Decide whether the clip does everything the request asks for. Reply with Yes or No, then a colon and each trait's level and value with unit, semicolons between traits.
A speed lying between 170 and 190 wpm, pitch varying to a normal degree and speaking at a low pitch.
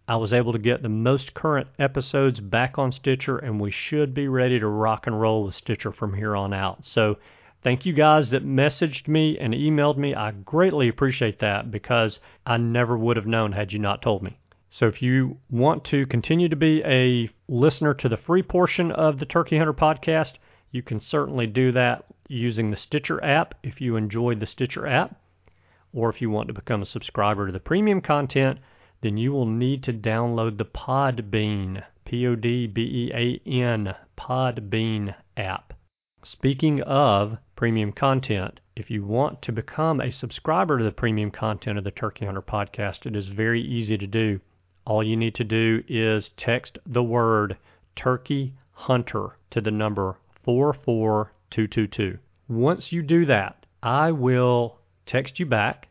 Yes: average, 175 wpm; average, 4.0 semitones; low, 120 Hz